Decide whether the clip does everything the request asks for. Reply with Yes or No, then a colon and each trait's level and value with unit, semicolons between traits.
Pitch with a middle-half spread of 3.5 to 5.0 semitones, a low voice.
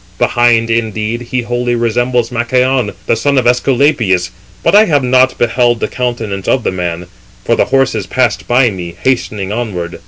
No: average, 2.8 semitones; low, 120 Hz